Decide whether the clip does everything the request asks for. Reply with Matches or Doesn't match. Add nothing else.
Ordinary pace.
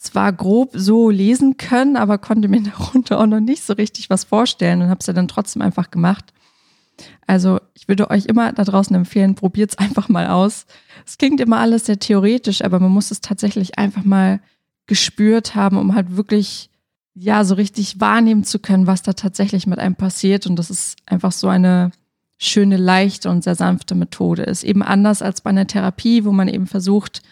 Doesn't match